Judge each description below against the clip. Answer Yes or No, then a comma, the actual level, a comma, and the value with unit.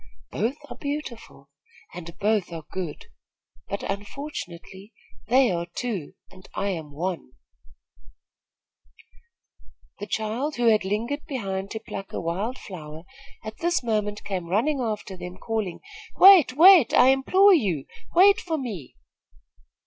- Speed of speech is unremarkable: No, slow, 130 wpm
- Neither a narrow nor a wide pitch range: No, wide, 6.4 semitones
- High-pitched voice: Yes, high, 210 Hz